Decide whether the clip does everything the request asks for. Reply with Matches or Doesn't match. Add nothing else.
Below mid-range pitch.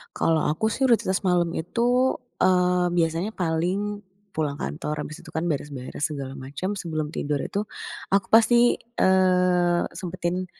Doesn't match